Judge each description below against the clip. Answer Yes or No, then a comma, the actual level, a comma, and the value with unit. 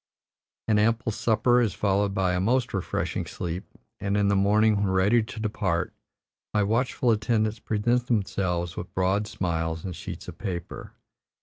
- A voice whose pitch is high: No, low, 105 Hz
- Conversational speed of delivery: Yes, average, 155 wpm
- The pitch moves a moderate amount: Yes, average, 3.0 semitones